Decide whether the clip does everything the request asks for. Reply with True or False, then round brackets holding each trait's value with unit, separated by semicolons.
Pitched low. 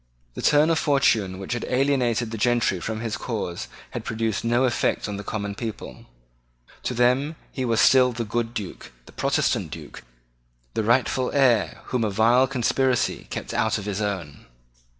True (115 Hz)